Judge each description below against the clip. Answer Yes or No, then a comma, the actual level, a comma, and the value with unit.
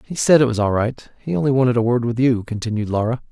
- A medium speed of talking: No, fast, 270 wpm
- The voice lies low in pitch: Yes, low, 120 Hz